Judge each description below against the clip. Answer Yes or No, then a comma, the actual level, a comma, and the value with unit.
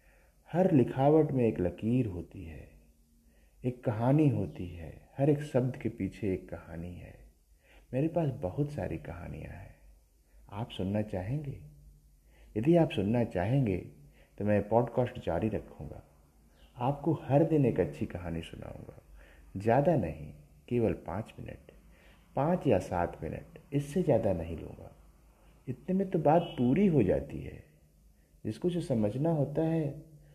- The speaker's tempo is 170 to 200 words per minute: No, average, 140 wpm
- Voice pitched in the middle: No, low, 105 Hz